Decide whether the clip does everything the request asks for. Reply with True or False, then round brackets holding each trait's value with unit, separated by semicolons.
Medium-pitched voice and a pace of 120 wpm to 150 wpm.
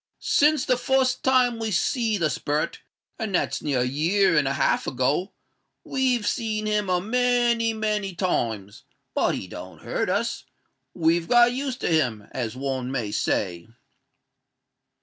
False (195 Hz; 140 wpm)